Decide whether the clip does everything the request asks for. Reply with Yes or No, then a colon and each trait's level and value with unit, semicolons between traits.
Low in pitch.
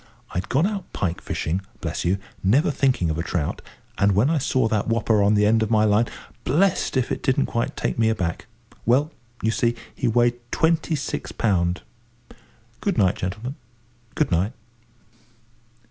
Yes: low, 115 Hz